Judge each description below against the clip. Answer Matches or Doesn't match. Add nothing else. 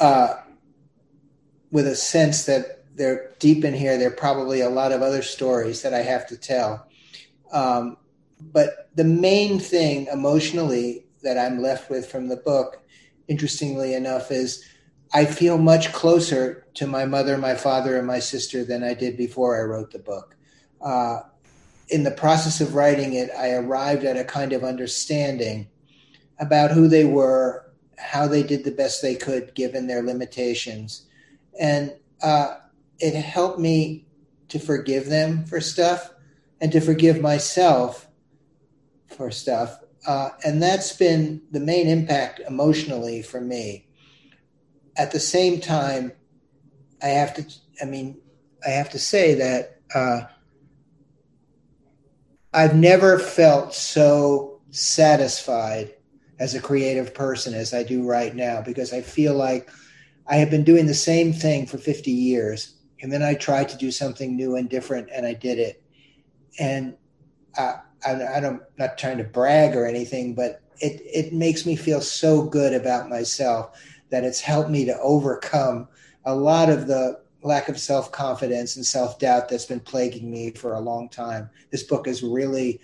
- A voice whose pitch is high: Doesn't match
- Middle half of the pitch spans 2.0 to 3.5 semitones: Matches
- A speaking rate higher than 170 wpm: Doesn't match